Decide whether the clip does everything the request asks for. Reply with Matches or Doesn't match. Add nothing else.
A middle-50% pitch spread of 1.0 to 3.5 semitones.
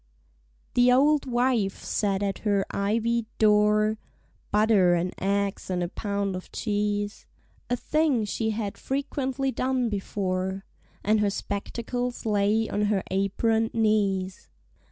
Matches